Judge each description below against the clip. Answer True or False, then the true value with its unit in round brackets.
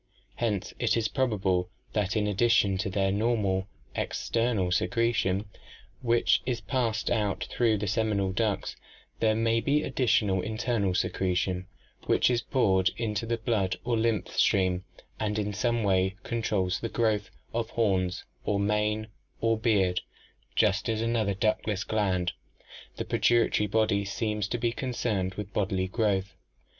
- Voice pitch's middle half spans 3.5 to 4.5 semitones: False (3.1 semitones)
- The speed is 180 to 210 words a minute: False (145 wpm)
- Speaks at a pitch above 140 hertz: False (105 Hz)